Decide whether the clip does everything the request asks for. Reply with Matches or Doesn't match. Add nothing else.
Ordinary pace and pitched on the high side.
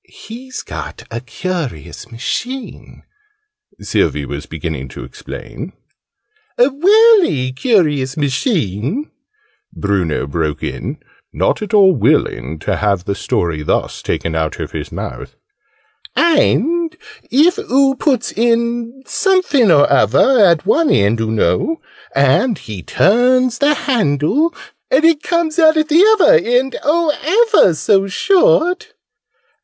Doesn't match